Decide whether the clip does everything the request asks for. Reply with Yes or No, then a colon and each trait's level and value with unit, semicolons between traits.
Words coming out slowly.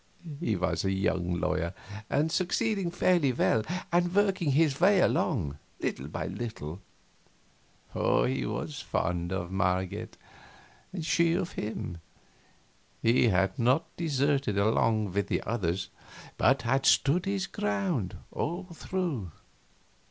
Yes: slow, 125 wpm